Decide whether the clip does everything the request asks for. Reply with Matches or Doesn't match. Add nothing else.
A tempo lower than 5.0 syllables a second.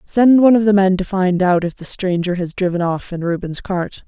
Doesn't match